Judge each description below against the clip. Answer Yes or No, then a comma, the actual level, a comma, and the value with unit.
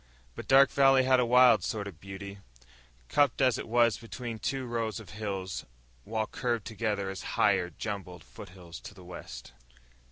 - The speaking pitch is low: Yes, low, 110 Hz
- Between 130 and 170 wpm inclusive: Yes, average, 165 wpm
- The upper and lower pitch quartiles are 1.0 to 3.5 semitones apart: No, average, 4.1 semitones